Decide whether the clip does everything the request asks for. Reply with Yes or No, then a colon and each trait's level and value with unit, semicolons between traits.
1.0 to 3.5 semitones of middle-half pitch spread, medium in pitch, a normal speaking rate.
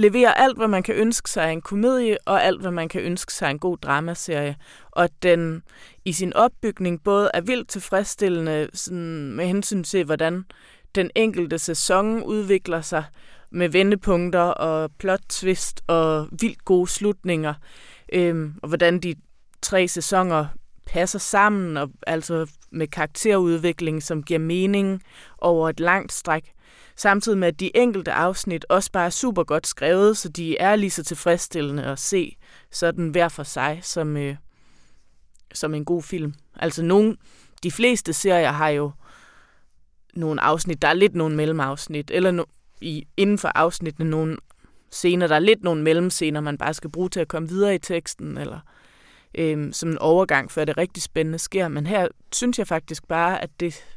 Yes: average, 3.2 semitones; medium, 170 Hz; average, 170 wpm